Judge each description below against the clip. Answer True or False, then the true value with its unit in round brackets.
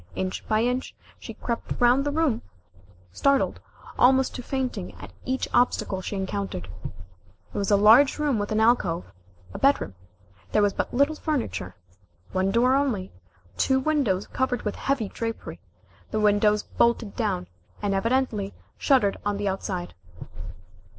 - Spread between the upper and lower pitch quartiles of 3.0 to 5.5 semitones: True (4.9 semitones)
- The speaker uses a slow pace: False (145 wpm)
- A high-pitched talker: True (225 Hz)